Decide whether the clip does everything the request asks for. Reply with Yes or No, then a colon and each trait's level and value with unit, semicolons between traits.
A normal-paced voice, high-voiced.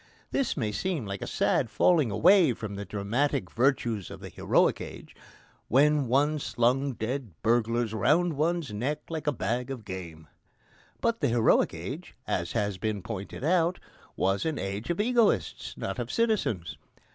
No: average, 155 wpm; low, 125 Hz